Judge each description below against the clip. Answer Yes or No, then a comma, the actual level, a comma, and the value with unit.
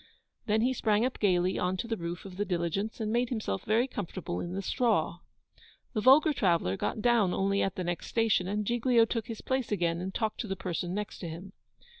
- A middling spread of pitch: Yes, average, 4.1 semitones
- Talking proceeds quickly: Yes, fast, 220 wpm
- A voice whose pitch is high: Yes, high, 205 Hz